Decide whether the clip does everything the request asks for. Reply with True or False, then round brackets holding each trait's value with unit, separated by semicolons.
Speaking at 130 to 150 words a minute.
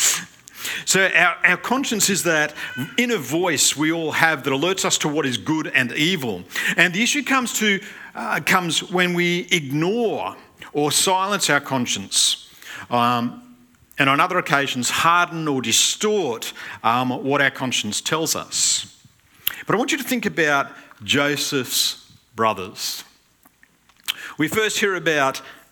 True (140 wpm)